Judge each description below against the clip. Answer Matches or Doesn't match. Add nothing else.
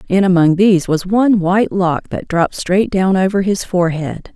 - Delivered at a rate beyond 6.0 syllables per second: Doesn't match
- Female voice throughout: Matches